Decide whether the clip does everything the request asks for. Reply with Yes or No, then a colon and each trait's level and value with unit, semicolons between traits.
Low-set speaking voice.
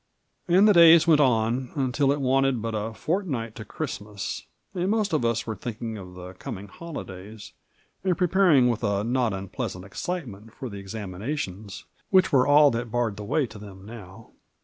Yes: low, 115 Hz